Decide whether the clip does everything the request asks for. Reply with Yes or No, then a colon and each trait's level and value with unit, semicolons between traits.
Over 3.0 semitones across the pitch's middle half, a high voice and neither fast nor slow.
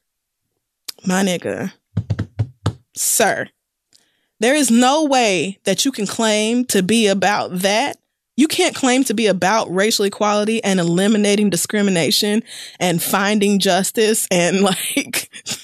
No: average, 3.7 semitones; high, 200 Hz; slow, 120 wpm